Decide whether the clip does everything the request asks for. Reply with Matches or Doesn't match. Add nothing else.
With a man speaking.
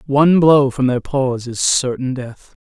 Matches